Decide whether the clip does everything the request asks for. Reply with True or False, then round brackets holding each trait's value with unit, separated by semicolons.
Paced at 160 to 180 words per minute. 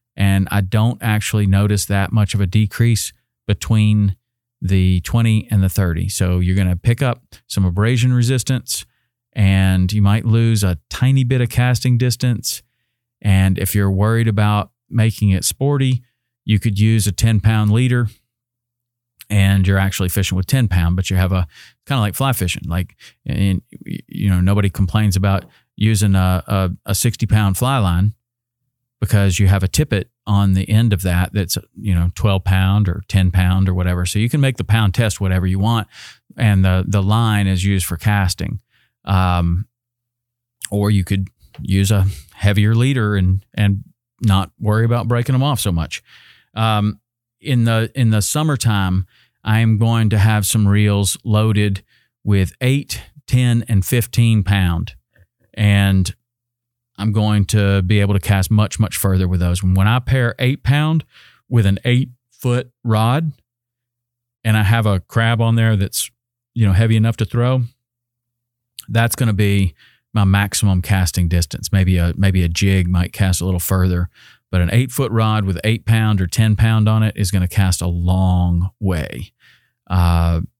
True (175 wpm)